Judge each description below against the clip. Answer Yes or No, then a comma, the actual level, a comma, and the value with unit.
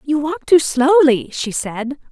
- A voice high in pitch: Yes, very high, 285 Hz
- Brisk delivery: No, average, 170 wpm